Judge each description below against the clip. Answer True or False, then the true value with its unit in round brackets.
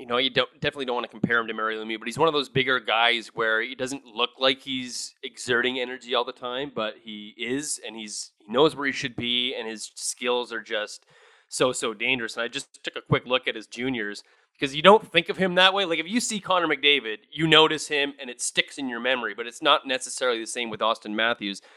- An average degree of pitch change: True (4.0 semitones)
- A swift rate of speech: True (255 wpm)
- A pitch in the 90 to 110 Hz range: False (125 Hz)